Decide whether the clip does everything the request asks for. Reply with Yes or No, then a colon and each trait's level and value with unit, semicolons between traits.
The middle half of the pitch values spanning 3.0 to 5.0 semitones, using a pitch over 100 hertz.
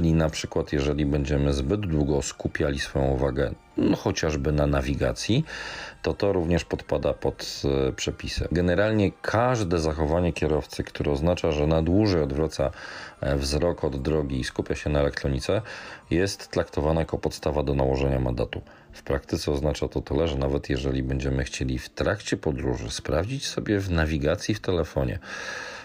No: average, 3.6 semitones; very low, 75 Hz